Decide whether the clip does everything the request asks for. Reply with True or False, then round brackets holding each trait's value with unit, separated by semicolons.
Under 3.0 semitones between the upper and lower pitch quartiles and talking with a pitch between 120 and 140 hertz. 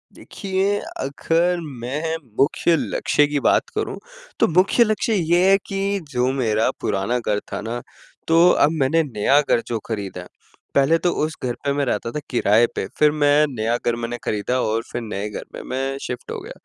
False (5.8 semitones; 135 Hz)